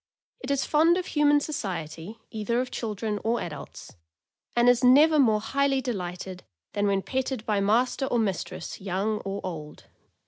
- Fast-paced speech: No, average, 160 wpm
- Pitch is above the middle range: Yes, high, 225 Hz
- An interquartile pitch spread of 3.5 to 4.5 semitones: No, average, 5.1 semitones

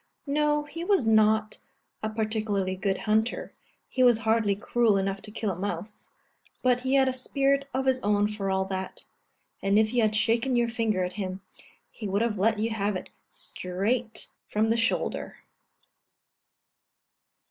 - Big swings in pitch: No, average, 3.3 semitones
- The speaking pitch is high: Yes, high, 220 Hz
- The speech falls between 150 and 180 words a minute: Yes, average, 165 wpm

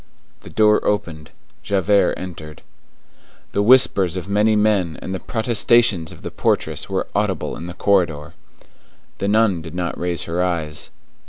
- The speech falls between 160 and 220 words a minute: No, average, 150 wpm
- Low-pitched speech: Yes, very low, 95 Hz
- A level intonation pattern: No, average, 3.7 semitones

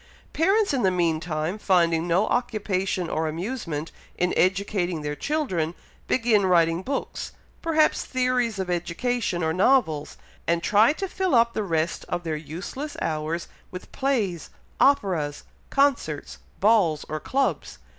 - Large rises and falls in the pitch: Yes, wide, 6.8 semitones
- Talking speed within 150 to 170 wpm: No, slow, 135 wpm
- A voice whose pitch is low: No, medium, 185 Hz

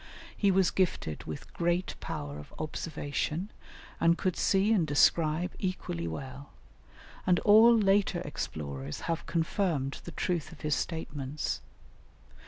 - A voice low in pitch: No, medium, 165 Hz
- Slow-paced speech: Yes, slow, 125 wpm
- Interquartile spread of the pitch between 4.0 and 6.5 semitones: Yes, average, 4.9 semitones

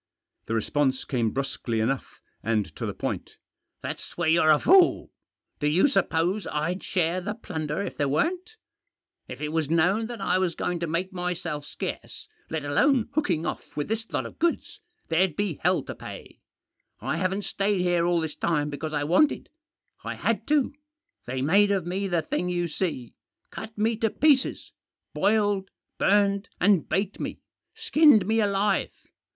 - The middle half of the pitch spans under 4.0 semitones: No, average, 4.9 semitones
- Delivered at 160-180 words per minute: Yes, average, 170 wpm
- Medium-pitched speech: Yes, medium, 180 Hz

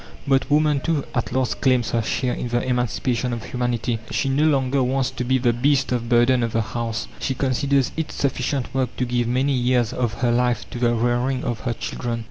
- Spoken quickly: Yes, fast, 215 wpm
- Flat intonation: Yes, narrow, 1.8 semitones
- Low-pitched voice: Yes, low, 125 Hz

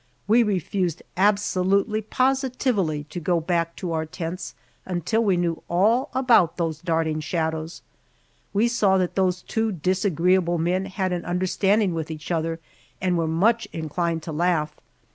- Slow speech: No, average, 145 wpm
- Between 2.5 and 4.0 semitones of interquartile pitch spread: Yes, average, 3.4 semitones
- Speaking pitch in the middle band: Yes, medium, 180 Hz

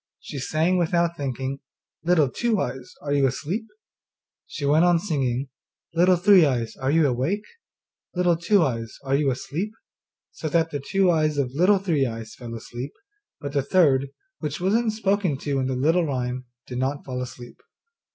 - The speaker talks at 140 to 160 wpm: No, average, 175 wpm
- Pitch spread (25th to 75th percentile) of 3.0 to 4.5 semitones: No, average, 5.1 semitones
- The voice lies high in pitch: No, medium, 145 Hz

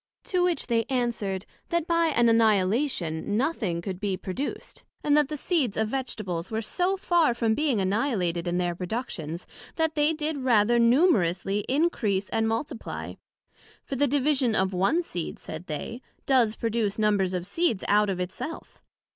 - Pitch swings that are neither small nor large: No, wide, 7.1 semitones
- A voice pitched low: No, high, 230 Hz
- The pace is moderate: Yes, average, 165 wpm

